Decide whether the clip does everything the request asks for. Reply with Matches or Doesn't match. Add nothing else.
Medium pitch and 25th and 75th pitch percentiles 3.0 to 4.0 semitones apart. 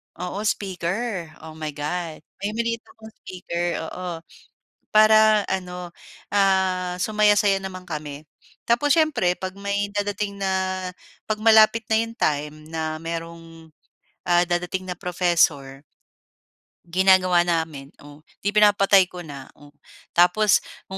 Matches